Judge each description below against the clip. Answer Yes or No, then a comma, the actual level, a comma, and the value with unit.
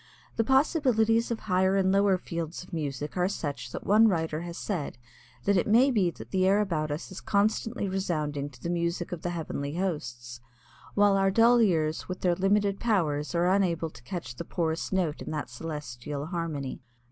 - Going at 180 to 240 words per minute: Yes, average, 190 wpm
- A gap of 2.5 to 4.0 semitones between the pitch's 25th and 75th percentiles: No, average, 4.6 semitones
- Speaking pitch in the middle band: Yes, medium, 175 Hz